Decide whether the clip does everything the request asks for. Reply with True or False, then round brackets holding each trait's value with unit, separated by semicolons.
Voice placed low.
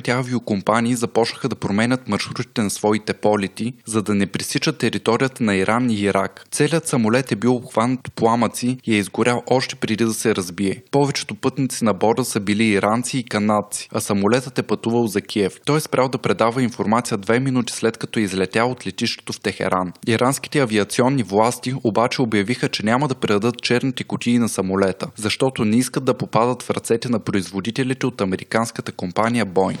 True (115 Hz)